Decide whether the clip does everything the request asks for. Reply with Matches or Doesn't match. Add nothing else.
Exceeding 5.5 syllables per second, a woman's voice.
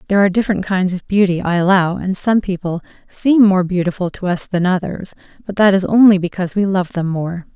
Matches